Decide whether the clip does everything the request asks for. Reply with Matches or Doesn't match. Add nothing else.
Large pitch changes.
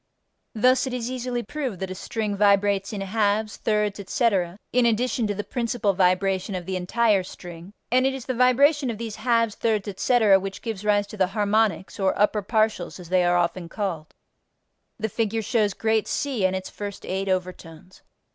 Doesn't match